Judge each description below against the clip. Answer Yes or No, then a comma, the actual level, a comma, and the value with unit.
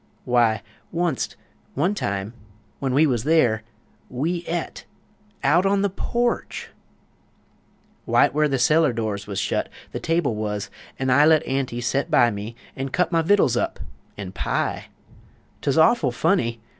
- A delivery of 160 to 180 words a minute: No, average, 145 wpm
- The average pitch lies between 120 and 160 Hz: Yes, low, 135 Hz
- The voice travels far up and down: Yes, wide, 6.1 semitones